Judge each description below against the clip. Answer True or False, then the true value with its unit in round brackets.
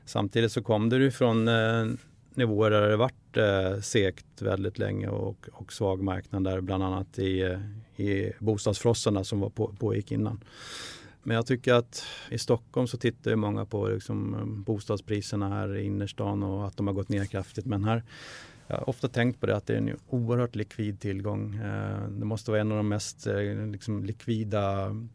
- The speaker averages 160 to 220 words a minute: True (175 wpm)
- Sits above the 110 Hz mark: False (105 Hz)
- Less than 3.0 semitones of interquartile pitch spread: True (2.6 semitones)